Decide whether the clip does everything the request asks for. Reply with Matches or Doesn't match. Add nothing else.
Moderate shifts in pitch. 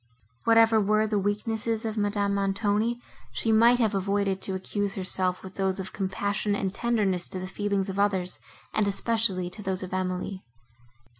Doesn't match